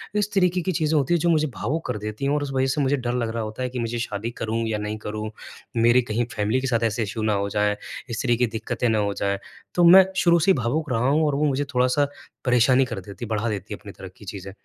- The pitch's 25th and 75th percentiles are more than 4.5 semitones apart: Yes, average, 5.0 semitones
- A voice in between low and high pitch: No, low, 120 Hz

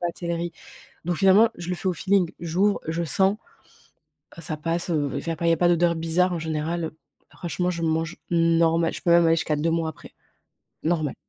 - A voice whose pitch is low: No, medium, 170 Hz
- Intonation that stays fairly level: Yes, narrow, 1.3 semitones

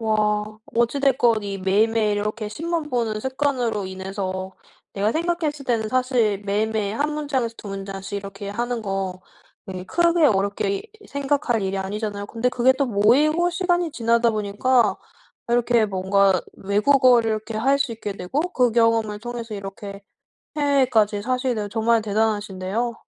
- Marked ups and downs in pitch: No, average, 4.0 semitones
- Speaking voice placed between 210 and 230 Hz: Yes, high, 220 Hz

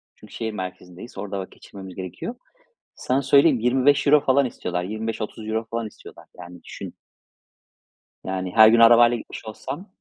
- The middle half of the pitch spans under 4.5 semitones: No, average, 5.1 semitones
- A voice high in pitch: No, low, 110 Hz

